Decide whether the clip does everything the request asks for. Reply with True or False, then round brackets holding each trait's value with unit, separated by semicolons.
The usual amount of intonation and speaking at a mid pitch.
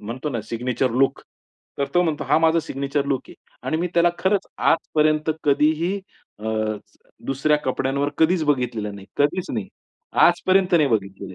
True (4.4 semitones; 145 Hz)